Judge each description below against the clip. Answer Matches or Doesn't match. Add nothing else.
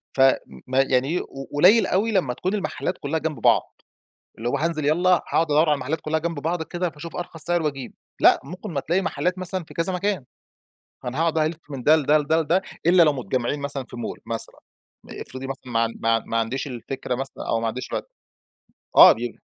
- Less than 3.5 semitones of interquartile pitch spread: Doesn't match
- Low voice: Doesn't match